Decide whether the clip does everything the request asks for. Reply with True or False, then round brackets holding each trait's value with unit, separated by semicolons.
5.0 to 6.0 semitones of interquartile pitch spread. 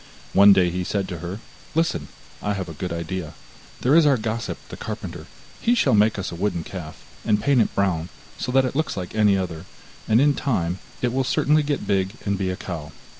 True (5.5 semitones)